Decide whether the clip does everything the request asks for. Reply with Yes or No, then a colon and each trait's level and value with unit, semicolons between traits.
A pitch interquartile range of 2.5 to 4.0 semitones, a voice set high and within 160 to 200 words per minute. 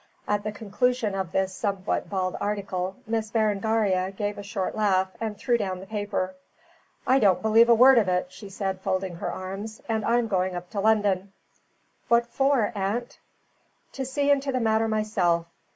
Yes: average, 2.9 semitones; high, 205 Hz; average, 175 wpm